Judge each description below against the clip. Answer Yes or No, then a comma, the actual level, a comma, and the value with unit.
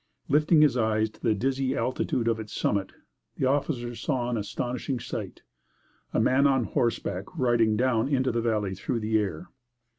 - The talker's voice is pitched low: Yes, low, 120 Hz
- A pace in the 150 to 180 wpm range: Yes, average, 170 wpm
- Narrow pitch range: No, average, 3.1 semitones